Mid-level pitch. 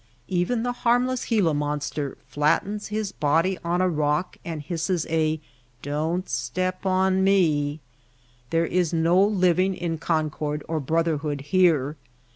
Yes: medium, 165 Hz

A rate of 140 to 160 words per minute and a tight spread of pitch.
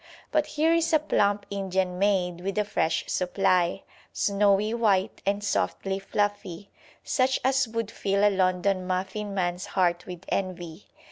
Yes: average, 145 wpm; narrow, 2.2 semitones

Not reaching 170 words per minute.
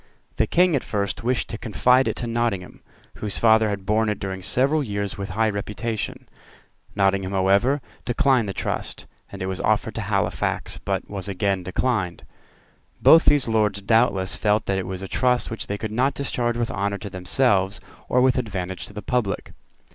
No: average, 185 wpm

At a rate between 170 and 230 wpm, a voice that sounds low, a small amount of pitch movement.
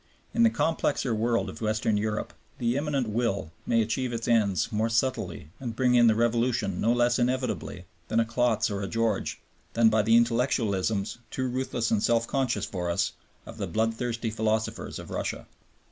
Yes: average, 175 wpm; low, 115 Hz; narrow, 2.0 semitones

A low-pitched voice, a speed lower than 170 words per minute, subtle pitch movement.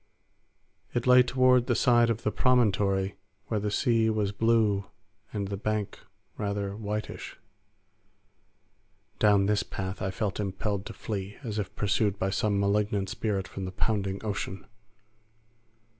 Yes: low, 105 Hz; average, 140 wpm; narrow, 2.1 semitones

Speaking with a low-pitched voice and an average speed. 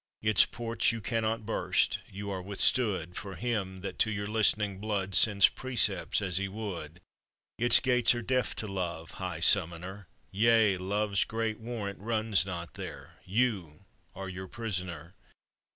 Yes: low, 100 Hz; average, 150 wpm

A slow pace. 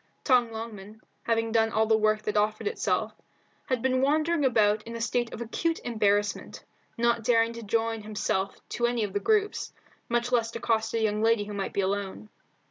No: average, 190 wpm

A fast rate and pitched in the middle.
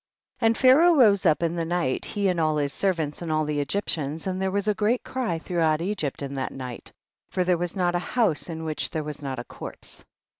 Yes: fast, 235 wpm; medium, 170 Hz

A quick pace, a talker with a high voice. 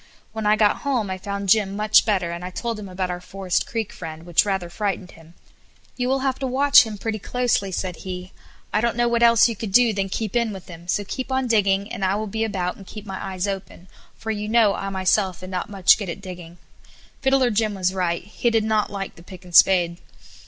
Yes: fast, 240 wpm; high, 200 Hz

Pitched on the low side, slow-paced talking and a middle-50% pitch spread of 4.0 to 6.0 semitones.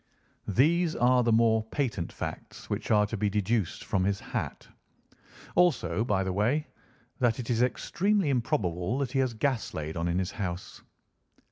No: low, 115 Hz; average, 165 wpm; average, 4.9 semitones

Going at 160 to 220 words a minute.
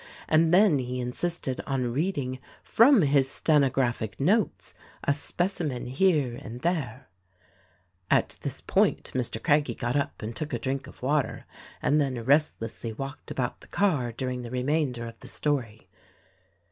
No: average, 150 wpm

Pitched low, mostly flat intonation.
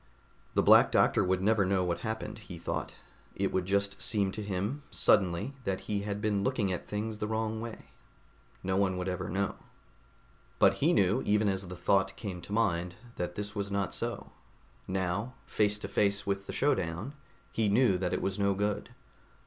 Yes: low, 100 Hz; narrow, 2.1 semitones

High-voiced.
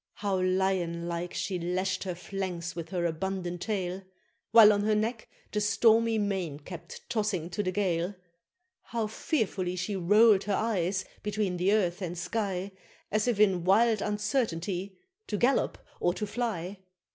Yes: high, 195 Hz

